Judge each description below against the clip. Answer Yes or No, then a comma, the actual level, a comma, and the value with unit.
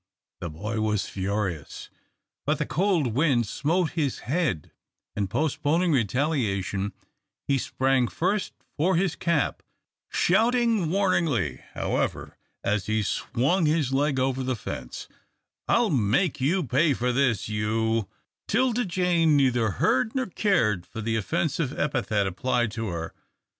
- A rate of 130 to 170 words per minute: Yes, slow, 135 wpm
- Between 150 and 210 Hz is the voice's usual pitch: No, low, 135 Hz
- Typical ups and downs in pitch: No, wide, 7.7 semitones